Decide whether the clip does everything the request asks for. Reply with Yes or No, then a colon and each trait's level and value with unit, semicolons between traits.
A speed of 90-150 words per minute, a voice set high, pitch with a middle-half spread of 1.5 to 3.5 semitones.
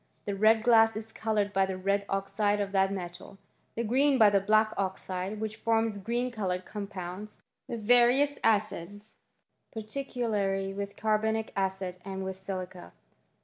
Yes: average, 145 wpm; high, 205 Hz; narrow, 2.4 semitones